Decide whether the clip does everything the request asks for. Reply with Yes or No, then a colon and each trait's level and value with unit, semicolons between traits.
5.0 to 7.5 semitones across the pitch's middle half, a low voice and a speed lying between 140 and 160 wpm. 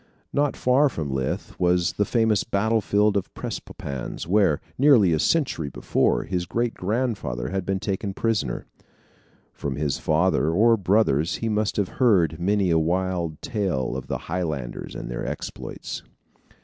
Yes: average, 5.3 semitones; very low, 95 Hz; average, 150 wpm